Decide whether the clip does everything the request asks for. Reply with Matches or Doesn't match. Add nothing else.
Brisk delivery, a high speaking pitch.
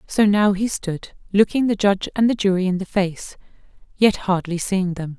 Doesn't match